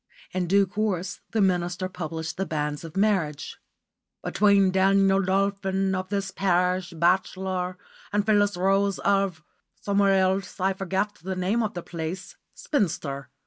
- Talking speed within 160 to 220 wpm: No, average, 140 wpm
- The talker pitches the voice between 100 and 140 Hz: No, high, 190 Hz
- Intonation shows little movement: Yes, narrow, 1.8 semitones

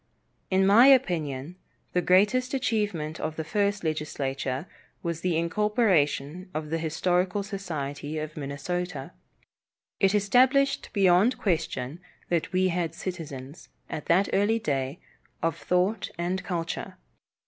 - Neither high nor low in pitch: Yes, medium, 175 Hz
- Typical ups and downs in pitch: Yes, average, 4.4 semitones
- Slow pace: Yes, slow, 120 wpm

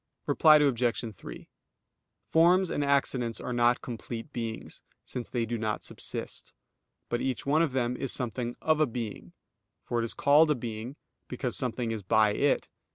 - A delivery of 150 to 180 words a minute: Yes, average, 165 wpm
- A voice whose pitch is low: Yes, low, 120 Hz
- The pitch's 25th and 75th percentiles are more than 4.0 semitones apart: No, average, 3.6 semitones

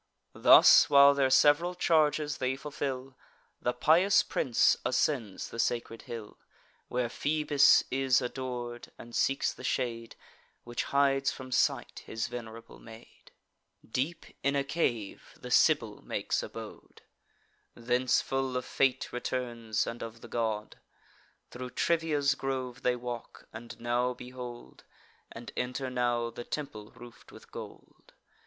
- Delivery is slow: Yes, slow, 130 wpm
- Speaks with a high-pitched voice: No, low, 125 Hz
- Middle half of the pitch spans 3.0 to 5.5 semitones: No, narrow, 2.5 semitones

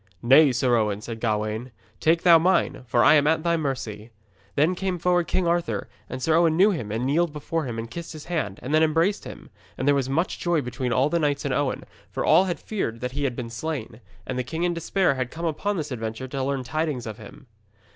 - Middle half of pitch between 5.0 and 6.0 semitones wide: Yes, wide, 5.4 semitones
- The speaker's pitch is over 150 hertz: No, medium, 145 Hz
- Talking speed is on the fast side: Yes, fast, 235 wpm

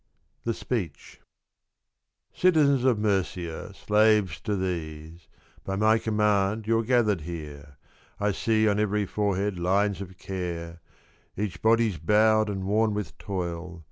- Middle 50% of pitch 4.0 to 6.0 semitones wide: No, average, 3.6 semitones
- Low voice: Yes, low, 100 Hz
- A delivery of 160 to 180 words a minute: No, average, 140 wpm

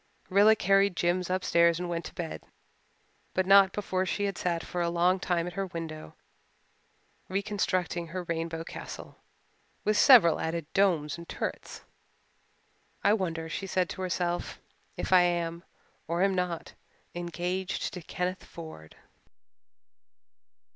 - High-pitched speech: No, medium, 180 Hz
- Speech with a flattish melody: Yes, narrow, 2.0 semitones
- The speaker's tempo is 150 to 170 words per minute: No, slow, 135 wpm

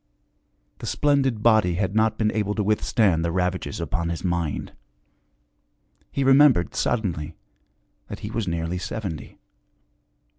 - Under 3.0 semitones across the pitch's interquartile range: No, average, 4.5 semitones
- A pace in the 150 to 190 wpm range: No, slow, 135 wpm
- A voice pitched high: No, low, 100 Hz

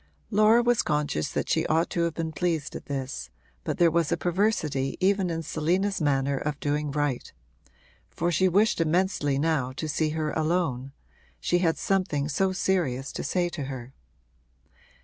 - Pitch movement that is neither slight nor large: Yes, average, 4.1 semitones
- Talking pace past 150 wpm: Yes, average, 170 wpm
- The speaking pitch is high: No, medium, 160 Hz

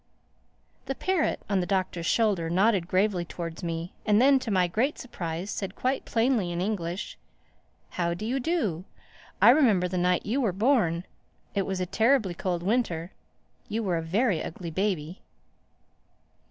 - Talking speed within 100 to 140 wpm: No, average, 160 wpm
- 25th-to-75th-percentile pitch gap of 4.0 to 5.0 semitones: Yes, average, 4.7 semitones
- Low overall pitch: No, high, 190 Hz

